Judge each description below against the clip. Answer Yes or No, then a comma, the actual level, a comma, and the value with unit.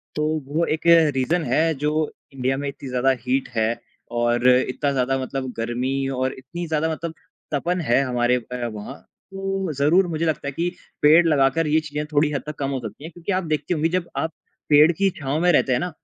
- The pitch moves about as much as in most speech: Yes, average, 3.8 semitones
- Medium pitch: Yes, medium, 145 Hz